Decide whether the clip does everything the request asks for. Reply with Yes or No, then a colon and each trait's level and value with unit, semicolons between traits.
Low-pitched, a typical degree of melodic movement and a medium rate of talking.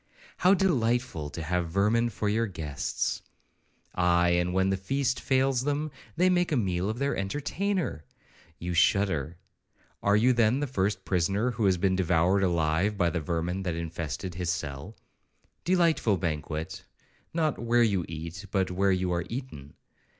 No: very low, 95 Hz; wide, 5.7 semitones; average, 150 wpm